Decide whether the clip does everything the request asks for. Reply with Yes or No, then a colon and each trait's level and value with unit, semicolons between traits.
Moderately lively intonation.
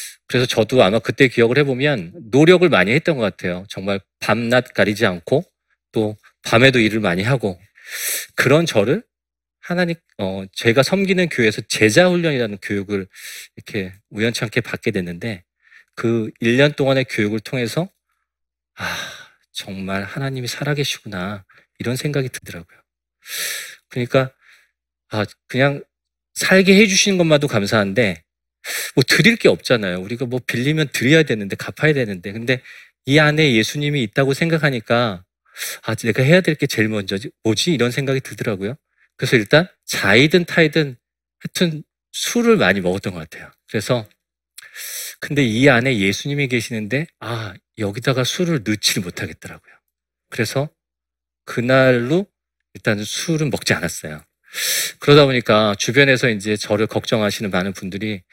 No: wide, 5.8 semitones